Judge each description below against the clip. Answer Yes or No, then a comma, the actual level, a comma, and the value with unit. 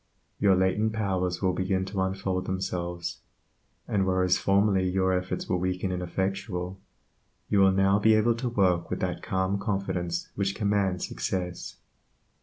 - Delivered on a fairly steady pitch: Yes, narrow, 1.4 semitones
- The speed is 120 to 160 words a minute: Yes, average, 150 wpm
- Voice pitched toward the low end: Yes, very low, 95 Hz